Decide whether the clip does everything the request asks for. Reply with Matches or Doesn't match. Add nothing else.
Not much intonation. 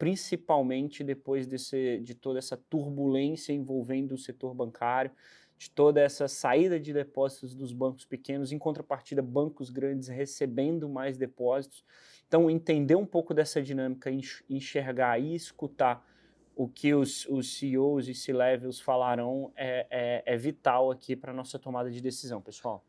Matches